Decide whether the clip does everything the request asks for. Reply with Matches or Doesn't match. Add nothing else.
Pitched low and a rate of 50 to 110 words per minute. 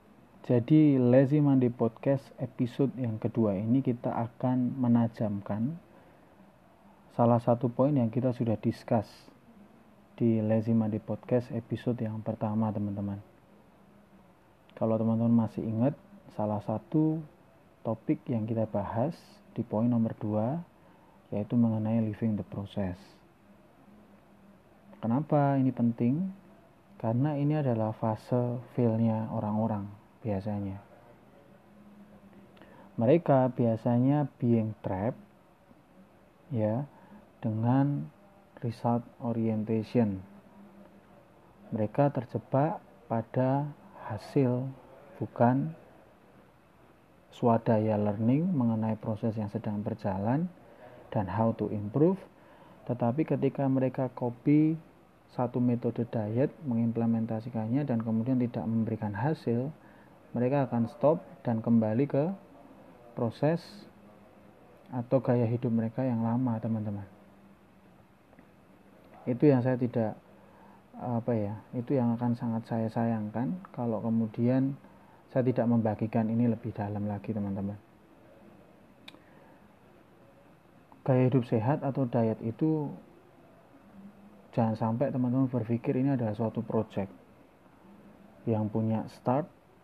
Matches